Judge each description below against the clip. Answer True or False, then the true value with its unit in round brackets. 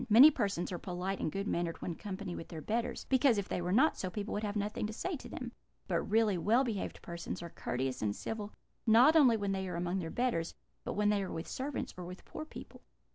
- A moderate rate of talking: False (245 wpm)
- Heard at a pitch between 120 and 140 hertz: False (200 Hz)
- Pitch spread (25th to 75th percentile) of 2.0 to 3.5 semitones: False (4.2 semitones)